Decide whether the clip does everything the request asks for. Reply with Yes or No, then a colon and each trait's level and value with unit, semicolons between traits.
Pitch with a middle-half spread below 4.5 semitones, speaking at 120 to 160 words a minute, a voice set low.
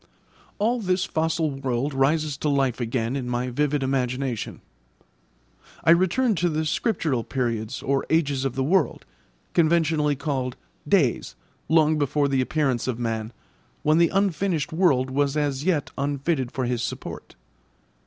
No: average, 3.7 semitones; average, 145 wpm; medium, 145 Hz